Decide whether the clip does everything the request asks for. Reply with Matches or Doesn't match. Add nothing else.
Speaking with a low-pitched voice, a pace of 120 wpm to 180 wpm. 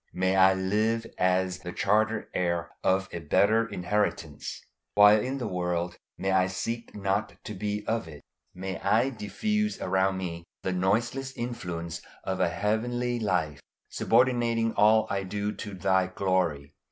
Matches